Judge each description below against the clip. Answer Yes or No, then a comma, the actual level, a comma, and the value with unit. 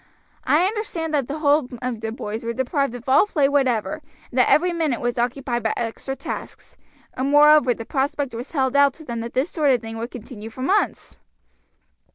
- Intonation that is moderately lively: Yes, average, 3.8 semitones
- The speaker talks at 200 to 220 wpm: Yes, fast, 205 wpm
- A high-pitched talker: Yes, very high, 265 Hz